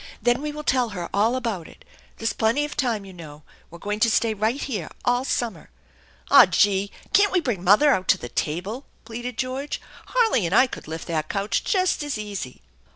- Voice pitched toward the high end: Yes, high, 220 Hz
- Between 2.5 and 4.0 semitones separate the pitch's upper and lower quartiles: No, average, 5.2 semitones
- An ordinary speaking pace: No, fast, 210 wpm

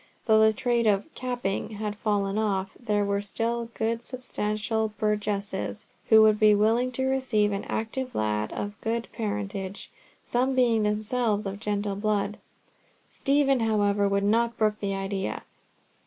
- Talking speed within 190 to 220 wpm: No, average, 145 wpm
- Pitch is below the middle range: No, high, 215 Hz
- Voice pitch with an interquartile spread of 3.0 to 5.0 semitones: No, narrow, 2.4 semitones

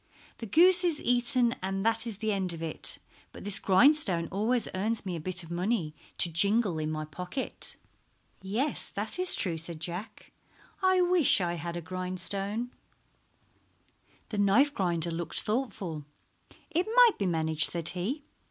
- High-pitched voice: Yes, high, 195 Hz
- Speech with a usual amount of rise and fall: No, wide, 5.8 semitones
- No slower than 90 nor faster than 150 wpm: No, average, 160 wpm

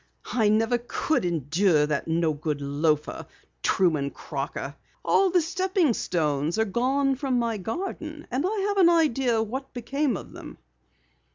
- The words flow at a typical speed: Yes, average, 150 wpm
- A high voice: Yes, high, 230 Hz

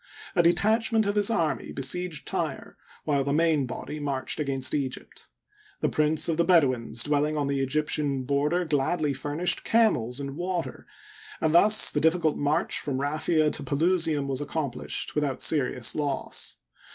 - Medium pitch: Yes, medium, 150 Hz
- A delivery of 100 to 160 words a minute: Yes, average, 155 wpm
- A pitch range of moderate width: Yes, average, 3.3 semitones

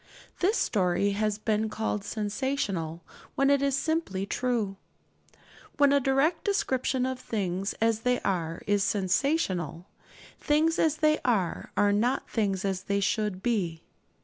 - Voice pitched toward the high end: Yes, high, 215 Hz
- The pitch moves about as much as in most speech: No, wide, 5.8 semitones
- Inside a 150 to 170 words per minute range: No, average, 140 wpm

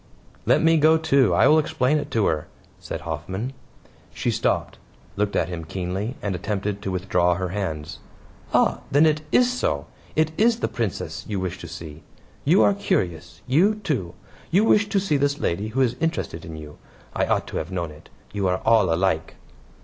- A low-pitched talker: Yes, low, 105 Hz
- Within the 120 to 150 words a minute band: No, average, 190 wpm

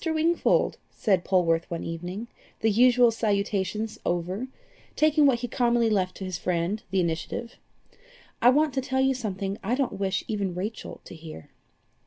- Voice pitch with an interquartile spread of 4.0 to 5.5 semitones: Yes, average, 5.1 semitones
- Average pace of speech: Yes, average, 160 wpm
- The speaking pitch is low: No, high, 210 Hz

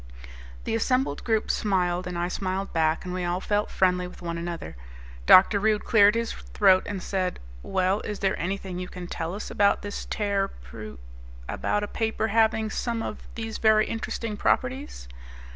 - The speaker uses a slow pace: No, average, 170 wpm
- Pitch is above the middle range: Yes, high, 200 Hz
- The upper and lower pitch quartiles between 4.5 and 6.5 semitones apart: No, average, 3.2 semitones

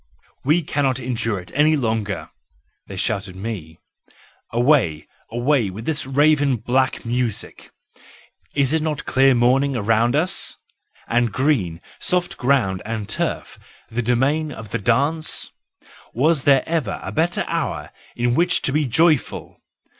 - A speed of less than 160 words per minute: Yes, average, 140 wpm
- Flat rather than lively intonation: No, average, 4.7 semitones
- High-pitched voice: No, low, 125 Hz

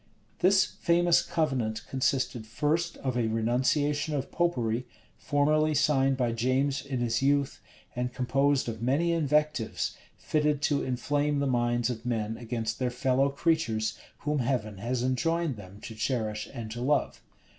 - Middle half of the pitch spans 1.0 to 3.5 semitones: No, average, 3.9 semitones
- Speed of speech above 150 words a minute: No, average, 145 wpm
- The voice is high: No, low, 130 Hz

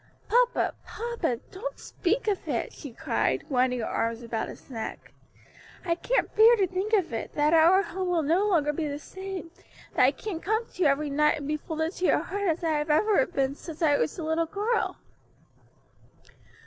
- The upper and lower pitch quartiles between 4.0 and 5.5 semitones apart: Yes, average, 5.1 semitones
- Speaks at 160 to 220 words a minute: Yes, average, 200 wpm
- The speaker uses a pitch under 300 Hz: No, very high, 330 Hz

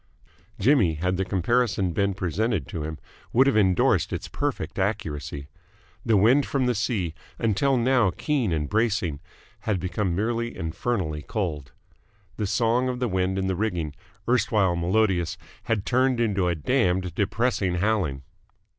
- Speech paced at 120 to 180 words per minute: Yes, average, 145 wpm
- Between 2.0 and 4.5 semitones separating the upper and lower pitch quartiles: No, average, 4.9 semitones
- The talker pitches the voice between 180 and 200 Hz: No, low, 100 Hz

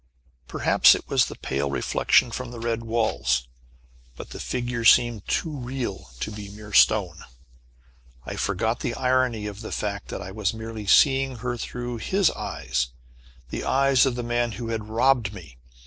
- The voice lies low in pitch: Yes, low, 115 Hz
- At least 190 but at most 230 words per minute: No, average, 170 wpm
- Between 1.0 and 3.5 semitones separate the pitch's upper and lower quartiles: Yes, average, 3.0 semitones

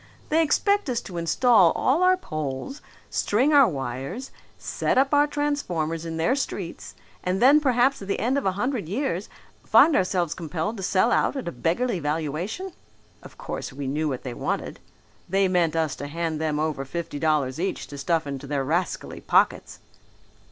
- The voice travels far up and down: Yes, wide, 8.6 semitones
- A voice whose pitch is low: No, medium, 180 Hz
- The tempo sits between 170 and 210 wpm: Yes, average, 180 wpm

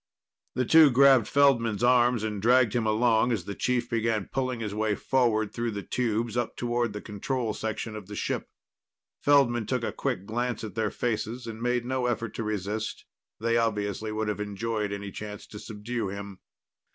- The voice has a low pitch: Yes, low, 115 Hz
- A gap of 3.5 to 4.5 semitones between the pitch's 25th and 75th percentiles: No, narrow, 2.5 semitones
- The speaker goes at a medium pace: Yes, average, 185 wpm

